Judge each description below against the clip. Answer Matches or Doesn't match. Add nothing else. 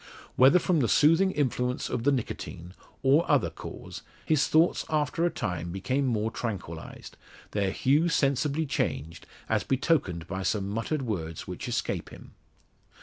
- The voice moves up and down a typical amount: Doesn't match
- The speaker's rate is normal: Matches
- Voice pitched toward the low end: Matches